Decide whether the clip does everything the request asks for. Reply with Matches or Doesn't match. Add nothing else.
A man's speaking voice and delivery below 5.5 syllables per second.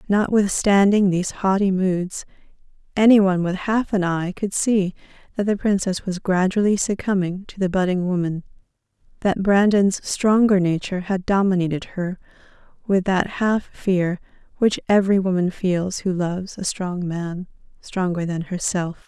Doesn't match